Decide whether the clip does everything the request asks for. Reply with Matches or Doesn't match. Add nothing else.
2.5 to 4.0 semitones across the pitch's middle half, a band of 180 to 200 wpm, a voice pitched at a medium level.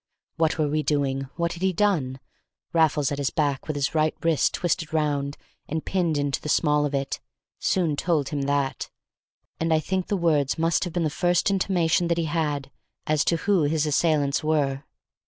Matches